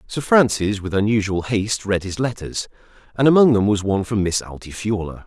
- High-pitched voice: No, low, 105 Hz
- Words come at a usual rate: Yes, average, 180 wpm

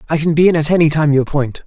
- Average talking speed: No, fast, 325 wpm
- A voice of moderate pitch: Yes, medium, 155 Hz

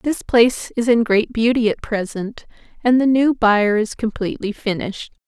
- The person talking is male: No, female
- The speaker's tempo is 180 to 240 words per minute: No, average, 170 wpm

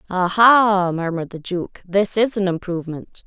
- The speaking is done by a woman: Yes, female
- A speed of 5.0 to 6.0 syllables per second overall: No, 4.6 syllables/s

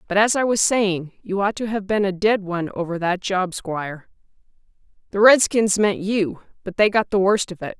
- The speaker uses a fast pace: Yes, fast, 215 wpm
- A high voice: Yes, high, 195 Hz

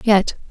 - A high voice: Yes, high, 205 Hz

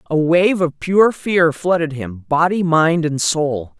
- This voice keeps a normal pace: Yes, average, 175 wpm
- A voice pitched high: No, medium, 170 Hz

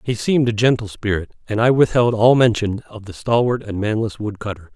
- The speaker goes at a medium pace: No, fast, 215 wpm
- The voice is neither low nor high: No, low, 110 Hz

